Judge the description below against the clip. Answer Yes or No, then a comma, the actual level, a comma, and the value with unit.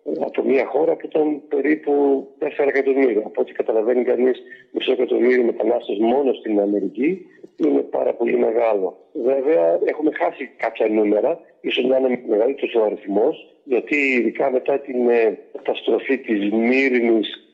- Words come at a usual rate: Yes, average, 135 wpm